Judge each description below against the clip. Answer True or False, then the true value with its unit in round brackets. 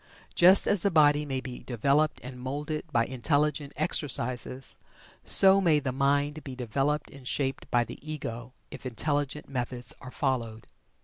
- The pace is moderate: True (150 wpm)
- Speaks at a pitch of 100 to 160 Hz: True (140 Hz)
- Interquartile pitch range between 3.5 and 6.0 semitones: False (2.9 semitones)